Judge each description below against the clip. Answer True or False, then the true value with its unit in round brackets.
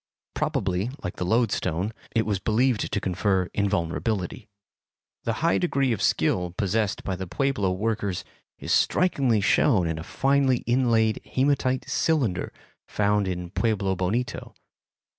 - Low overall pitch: True (105 Hz)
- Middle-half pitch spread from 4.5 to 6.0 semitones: True (4.8 semitones)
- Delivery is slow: True (130 wpm)